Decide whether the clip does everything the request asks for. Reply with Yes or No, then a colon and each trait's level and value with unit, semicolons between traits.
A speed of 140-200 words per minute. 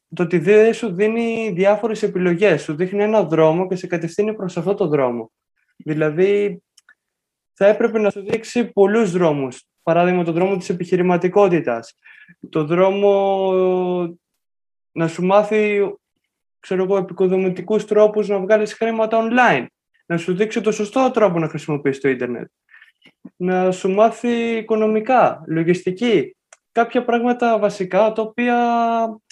No: average, 125 wpm